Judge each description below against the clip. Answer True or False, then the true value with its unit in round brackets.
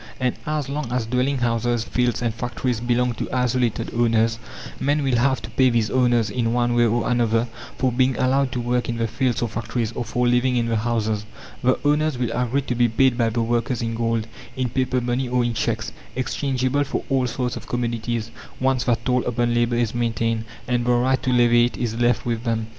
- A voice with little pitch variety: True (1.6 semitones)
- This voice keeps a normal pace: False (215 wpm)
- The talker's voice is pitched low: True (120 Hz)